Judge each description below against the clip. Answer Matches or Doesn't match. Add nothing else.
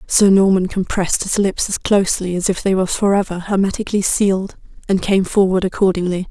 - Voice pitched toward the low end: Doesn't match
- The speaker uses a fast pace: Doesn't match